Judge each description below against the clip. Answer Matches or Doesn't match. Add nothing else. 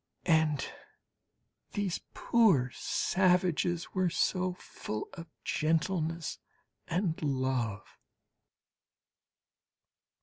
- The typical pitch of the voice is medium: Matches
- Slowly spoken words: Matches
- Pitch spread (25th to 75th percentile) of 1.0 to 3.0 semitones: Doesn't match